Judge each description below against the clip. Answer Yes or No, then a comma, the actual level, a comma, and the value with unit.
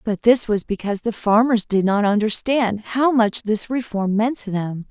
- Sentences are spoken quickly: No, average, 195 wpm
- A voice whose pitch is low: No, high, 220 Hz